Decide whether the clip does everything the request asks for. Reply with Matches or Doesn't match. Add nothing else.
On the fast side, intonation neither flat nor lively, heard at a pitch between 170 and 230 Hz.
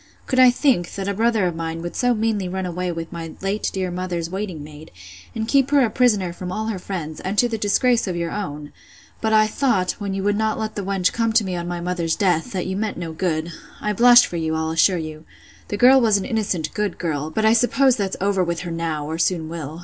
Matches